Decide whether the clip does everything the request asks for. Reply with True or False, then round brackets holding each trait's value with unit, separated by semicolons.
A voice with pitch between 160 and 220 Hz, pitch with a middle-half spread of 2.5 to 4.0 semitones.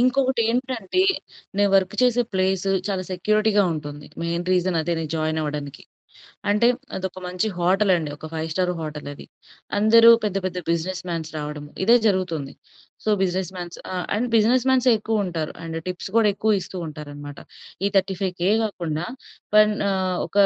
False (185 Hz; 4.6 semitones)